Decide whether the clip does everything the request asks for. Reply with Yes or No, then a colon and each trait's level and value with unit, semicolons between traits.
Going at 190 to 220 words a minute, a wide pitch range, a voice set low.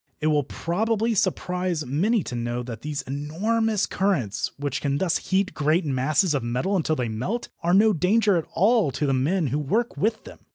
No: average, 195 wpm; wide, 6.2 semitones; medium, 165 Hz